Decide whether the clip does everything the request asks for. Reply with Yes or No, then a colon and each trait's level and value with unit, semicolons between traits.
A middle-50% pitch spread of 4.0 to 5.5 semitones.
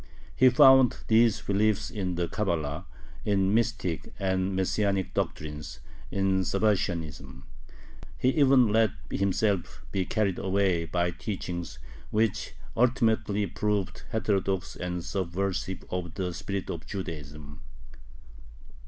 No: average, 3.6 semitones